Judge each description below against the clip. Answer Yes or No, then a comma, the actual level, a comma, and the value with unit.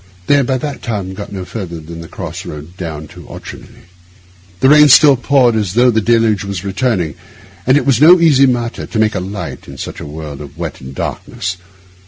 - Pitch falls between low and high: No, low, 105 Hz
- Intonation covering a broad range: Yes, wide, 6.8 semitones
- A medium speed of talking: No, fast, 215 wpm